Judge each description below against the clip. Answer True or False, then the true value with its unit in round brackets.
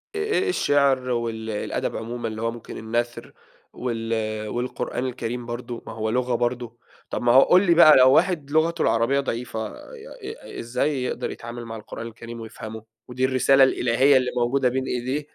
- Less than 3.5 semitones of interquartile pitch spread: True (2.5 semitones)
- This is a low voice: True (125 Hz)